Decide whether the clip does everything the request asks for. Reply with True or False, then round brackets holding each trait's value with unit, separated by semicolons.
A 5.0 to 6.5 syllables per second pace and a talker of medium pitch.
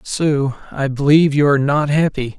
True (5.2 syllables/s; 145 Hz)